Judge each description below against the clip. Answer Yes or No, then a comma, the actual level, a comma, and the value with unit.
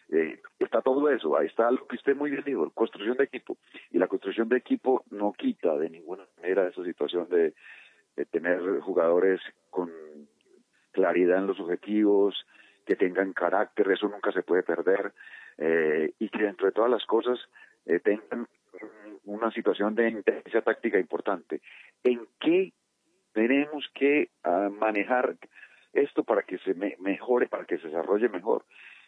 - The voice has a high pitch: No, low, 125 Hz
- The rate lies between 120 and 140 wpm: No, average, 155 wpm